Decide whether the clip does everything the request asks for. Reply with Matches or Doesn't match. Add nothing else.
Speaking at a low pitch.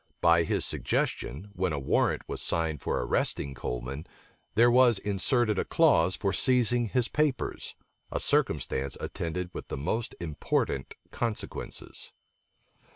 Matches